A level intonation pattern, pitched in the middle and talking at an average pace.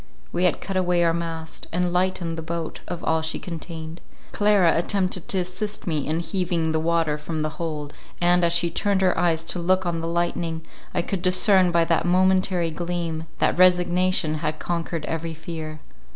Yes: narrow, 1.9 semitones; medium, 170 Hz; average, 180 wpm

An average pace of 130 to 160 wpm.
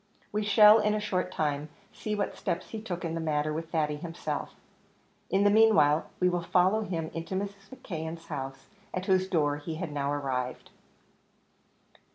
No: average, 175 wpm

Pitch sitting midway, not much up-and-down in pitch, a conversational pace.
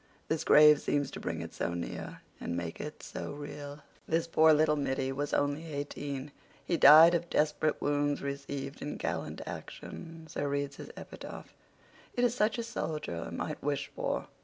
Yes: medium, 145 Hz; narrow, 2.0 semitones; average, 170 wpm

